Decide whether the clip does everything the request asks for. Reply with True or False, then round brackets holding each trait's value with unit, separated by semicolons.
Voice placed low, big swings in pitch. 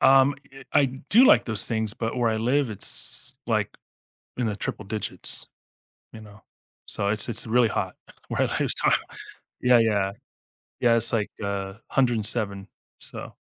False (115 Hz; 2.6 semitones)